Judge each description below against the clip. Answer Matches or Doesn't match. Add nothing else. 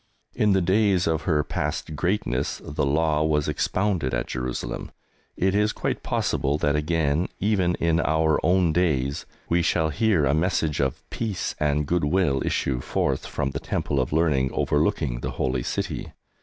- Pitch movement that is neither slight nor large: Matches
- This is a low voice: Matches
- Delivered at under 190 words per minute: Matches